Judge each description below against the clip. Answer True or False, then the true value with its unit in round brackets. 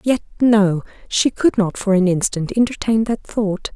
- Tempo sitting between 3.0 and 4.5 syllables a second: True (4.4 syllables/s)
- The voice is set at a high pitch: True (210 Hz)